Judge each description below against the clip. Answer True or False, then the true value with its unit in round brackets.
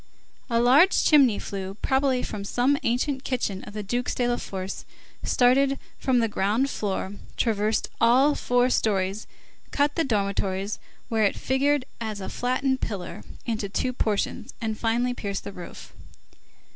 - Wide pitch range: False (4.2 semitones)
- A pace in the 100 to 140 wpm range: False (150 wpm)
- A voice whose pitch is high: True (230 Hz)